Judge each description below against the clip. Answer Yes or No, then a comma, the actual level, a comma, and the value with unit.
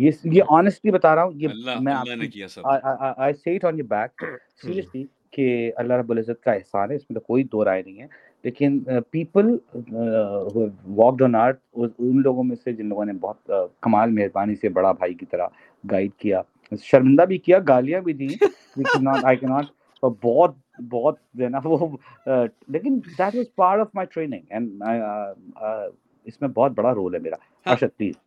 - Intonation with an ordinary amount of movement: No, wide, 5.9 semitones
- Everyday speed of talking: Yes, average, 180 wpm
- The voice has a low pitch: Yes, low, 130 Hz